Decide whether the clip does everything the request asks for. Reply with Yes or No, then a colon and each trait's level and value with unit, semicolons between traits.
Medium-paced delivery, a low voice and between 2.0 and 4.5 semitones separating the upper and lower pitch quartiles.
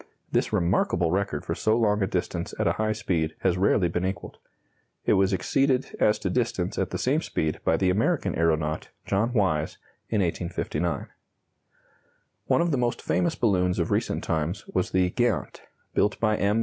Yes: average, 175 wpm; very low, 95 Hz; average, 3.8 semitones